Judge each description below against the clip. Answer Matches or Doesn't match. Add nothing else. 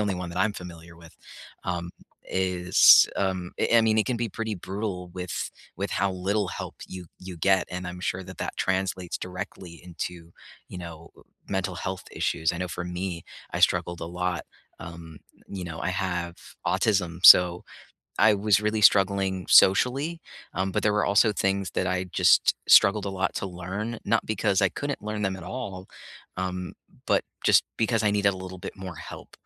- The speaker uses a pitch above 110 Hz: Doesn't match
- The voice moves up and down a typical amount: Doesn't match